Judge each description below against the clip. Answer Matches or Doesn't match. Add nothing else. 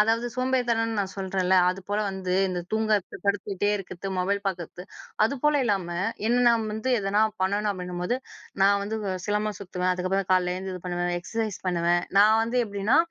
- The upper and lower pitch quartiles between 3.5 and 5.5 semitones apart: Doesn't match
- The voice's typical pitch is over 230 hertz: Doesn't match